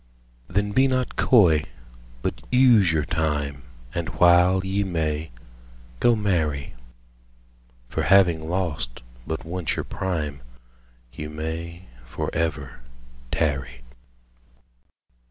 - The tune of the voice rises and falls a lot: No, average, 3.8 semitones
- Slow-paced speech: Yes, slow, 105 wpm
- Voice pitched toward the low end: Yes, very low, 85 Hz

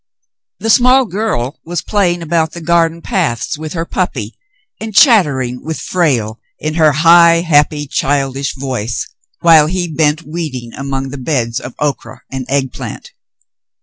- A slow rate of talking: No, average, 150 wpm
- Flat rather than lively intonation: No, average, 4.2 semitones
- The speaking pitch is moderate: Yes, medium, 155 Hz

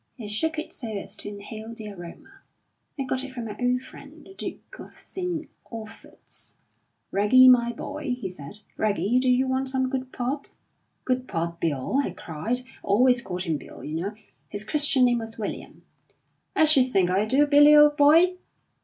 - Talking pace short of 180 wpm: No, average, 185 wpm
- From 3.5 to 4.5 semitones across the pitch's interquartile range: No, average, 5.2 semitones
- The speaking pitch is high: Yes, very high, 250 Hz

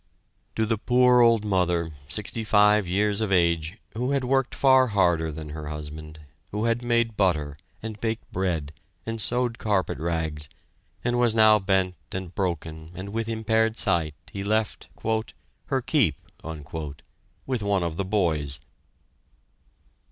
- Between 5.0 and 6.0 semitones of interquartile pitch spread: Yes, wide, 5.5 semitones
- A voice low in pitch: Yes, low, 100 Hz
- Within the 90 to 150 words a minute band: Yes, average, 145 wpm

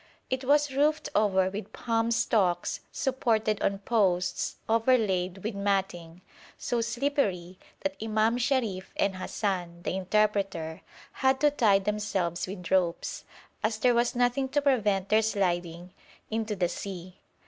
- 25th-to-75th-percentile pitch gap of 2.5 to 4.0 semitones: No, average, 4.4 semitones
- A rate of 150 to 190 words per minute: No, slow, 135 wpm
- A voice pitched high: Yes, high, 210 Hz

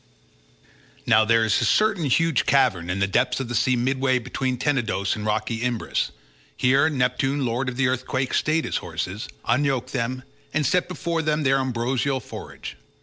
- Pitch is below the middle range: Yes, low, 130 Hz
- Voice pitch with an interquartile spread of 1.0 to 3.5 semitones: Yes, average, 3.0 semitones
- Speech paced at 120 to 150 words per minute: No, average, 170 wpm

